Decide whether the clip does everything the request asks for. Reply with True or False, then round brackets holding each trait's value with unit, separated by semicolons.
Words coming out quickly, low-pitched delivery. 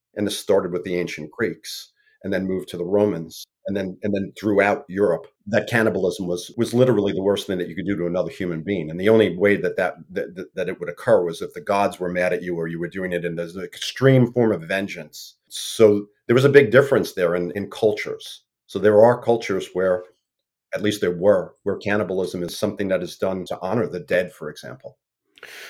True (225 wpm; 95 Hz)